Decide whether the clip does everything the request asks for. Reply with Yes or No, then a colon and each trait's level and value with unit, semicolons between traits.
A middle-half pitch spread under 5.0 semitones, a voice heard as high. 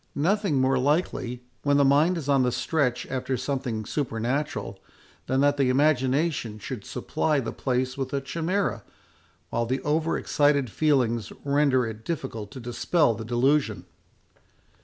No: average, 3.2 semitones; low, 135 Hz